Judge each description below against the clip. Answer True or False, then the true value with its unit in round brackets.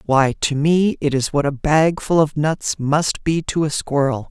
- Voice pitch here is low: False (150 Hz)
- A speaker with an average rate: False (225 wpm)